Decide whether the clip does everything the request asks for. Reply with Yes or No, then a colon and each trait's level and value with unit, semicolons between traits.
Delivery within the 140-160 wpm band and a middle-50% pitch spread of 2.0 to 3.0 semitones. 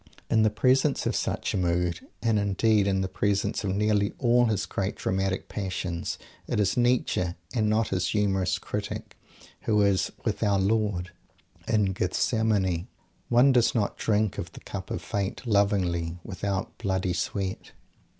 Yes: average, 155 wpm; narrow, 2.6 semitones